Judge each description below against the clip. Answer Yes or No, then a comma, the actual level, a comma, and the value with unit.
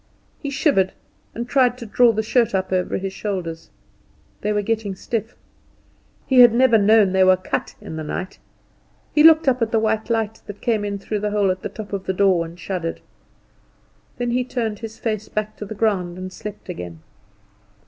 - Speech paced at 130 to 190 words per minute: No, average, 200 wpm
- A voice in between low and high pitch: No, high, 210 Hz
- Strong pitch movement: No, average, 3.3 semitones